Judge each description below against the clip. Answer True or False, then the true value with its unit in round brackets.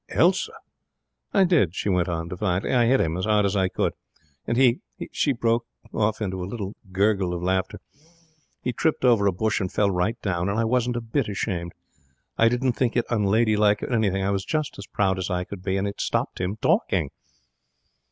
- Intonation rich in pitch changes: False (3.8 semitones)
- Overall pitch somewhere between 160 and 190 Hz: False (105 Hz)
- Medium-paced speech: False (210 wpm)